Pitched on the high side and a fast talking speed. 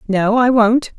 No: high, 225 Hz; average, 185 wpm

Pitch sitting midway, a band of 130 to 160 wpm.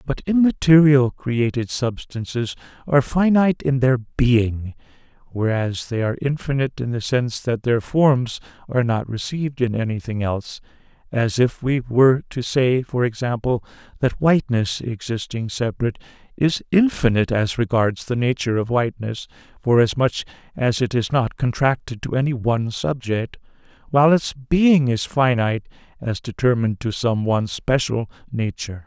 No: low, 125 Hz; average, 140 wpm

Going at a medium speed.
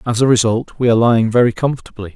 No: fast, 225 wpm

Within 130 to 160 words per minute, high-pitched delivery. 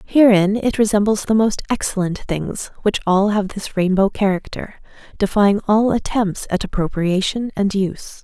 Yes: average, 145 wpm; high, 200 Hz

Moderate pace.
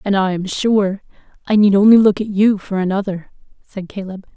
Yes: average, 180 wpm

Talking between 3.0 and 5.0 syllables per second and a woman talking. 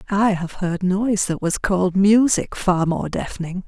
Yes: 4.6 syllables/s; female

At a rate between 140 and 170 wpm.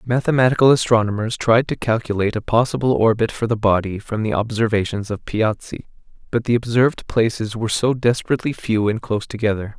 Yes: average, 165 wpm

